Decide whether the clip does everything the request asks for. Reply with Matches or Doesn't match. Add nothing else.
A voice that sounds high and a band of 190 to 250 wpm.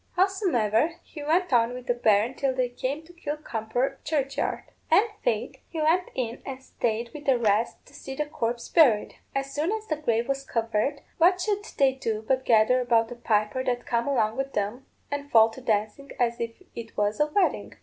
Matches